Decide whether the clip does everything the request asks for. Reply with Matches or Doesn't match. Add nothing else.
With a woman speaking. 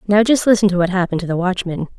Matches